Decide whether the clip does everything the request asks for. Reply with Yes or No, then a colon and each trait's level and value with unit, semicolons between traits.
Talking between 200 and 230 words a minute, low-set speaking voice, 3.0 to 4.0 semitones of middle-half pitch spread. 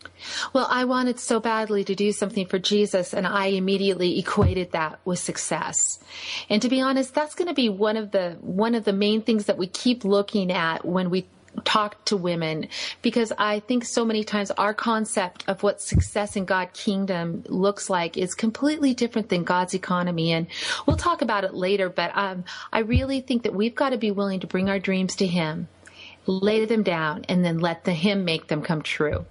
No: fast, 205 wpm; high, 200 Hz; average, 3.5 semitones